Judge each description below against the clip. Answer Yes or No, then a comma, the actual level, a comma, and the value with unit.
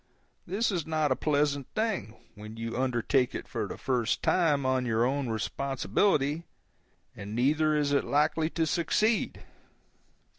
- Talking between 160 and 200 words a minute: No, average, 145 wpm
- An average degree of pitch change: Yes, average, 4.1 semitones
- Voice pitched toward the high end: No, medium, 140 Hz